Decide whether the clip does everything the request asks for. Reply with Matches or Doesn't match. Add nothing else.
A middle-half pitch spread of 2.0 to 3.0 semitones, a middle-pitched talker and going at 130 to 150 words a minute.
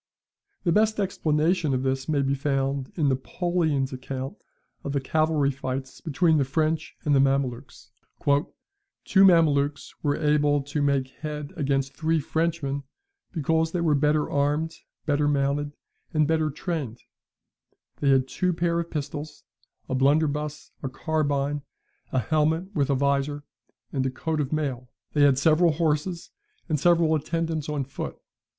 Matches